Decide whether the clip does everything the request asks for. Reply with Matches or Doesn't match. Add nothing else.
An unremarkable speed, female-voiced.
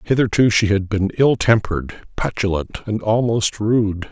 Doesn't match